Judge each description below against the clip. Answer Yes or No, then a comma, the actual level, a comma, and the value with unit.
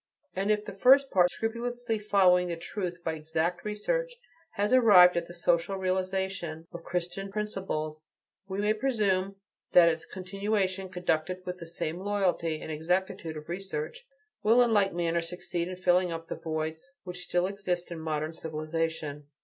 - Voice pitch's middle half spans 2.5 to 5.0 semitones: Yes, average, 3.1 semitones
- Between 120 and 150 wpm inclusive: No, average, 160 wpm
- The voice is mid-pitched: Yes, medium, 180 Hz